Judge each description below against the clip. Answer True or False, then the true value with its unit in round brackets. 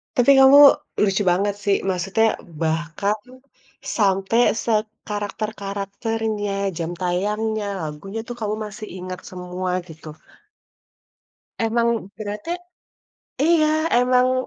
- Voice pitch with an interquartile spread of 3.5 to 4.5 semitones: False (2.9 semitones)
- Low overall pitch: False (205 Hz)